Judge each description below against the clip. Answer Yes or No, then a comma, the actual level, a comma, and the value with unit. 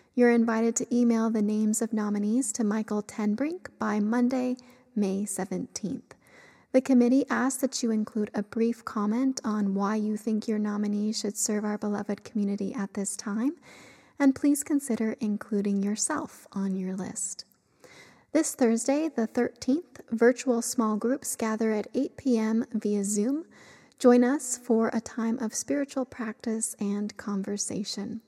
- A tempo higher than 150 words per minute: No, average, 145 wpm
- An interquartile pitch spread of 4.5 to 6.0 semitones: No, average, 3.1 semitones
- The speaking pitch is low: No, high, 225 Hz